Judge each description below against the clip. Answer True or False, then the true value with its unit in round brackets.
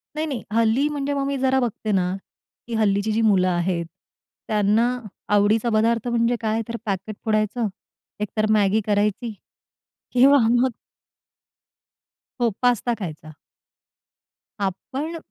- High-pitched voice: True (220 Hz)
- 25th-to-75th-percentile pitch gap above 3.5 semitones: False (3.1 semitones)